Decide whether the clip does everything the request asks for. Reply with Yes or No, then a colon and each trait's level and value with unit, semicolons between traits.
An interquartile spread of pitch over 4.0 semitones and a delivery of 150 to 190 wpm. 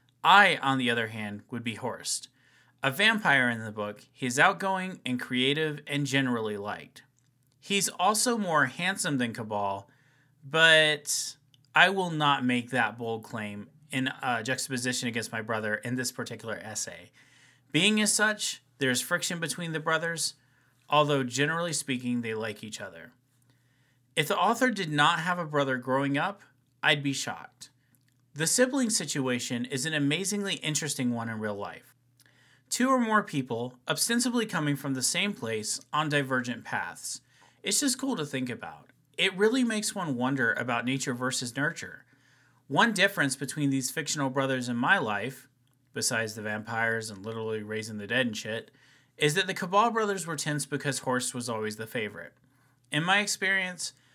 Yes: average, 4.6 semitones; average, 160 wpm